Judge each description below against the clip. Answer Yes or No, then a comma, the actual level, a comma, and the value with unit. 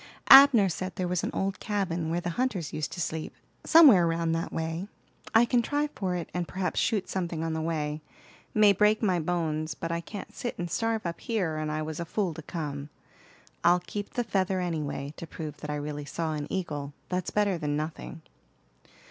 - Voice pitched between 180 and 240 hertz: No, medium, 170 Hz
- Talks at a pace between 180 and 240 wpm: Yes, fast, 205 wpm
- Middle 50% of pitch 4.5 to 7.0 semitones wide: No, average, 3.8 semitones